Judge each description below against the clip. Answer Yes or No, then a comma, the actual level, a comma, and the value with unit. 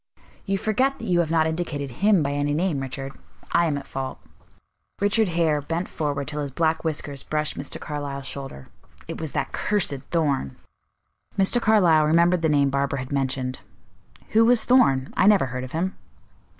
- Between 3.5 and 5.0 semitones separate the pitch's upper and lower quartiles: Yes, average, 4.3 semitones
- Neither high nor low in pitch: Yes, medium, 155 Hz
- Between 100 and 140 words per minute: No, average, 175 wpm